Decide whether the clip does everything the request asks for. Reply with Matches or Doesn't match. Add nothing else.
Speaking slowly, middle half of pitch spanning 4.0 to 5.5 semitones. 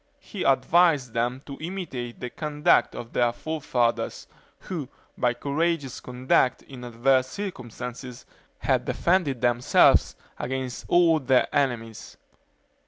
Matches